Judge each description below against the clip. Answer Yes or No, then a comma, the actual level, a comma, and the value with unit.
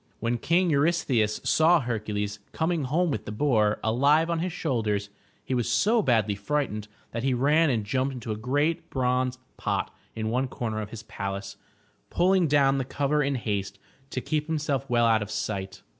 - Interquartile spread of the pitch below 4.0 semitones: No, wide, 5.5 semitones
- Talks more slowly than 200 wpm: Yes, average, 180 wpm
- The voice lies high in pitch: No, low, 125 Hz